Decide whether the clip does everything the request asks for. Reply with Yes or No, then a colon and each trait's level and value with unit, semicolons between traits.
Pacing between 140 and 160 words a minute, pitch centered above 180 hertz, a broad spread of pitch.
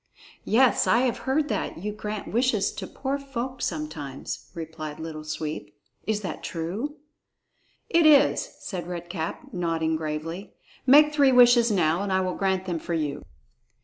Yes: average, 155 wpm; high, 190 Hz; wide, 7.4 semitones